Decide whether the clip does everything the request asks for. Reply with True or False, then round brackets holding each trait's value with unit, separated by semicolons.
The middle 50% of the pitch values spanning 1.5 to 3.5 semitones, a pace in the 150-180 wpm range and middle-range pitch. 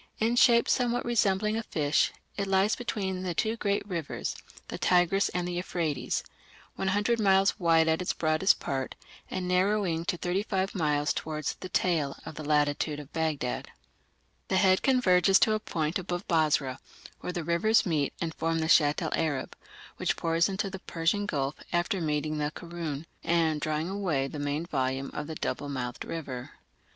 False (4.1 semitones; 170 wpm; 170 Hz)